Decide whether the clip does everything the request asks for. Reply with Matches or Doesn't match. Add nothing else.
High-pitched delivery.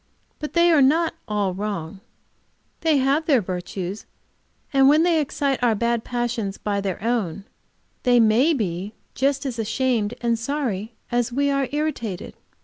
Matches